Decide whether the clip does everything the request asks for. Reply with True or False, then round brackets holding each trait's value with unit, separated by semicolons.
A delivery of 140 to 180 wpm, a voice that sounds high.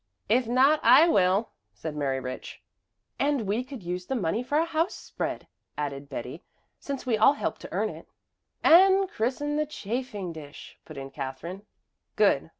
True (165 wpm; 215 Hz)